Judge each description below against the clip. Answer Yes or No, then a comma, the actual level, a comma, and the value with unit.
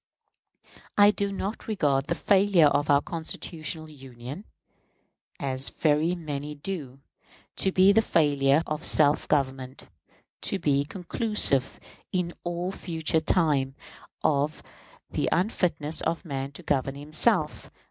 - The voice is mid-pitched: Yes, medium, 155 Hz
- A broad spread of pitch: No, average, 4.2 semitones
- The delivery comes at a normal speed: No, slow, 120 wpm